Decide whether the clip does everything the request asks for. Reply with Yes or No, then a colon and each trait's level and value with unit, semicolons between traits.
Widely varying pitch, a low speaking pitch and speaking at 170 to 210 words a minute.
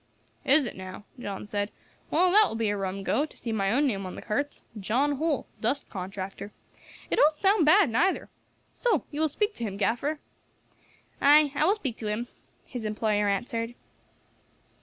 No: wide, 6.6 semitones; high, 240 Hz; average, 180 wpm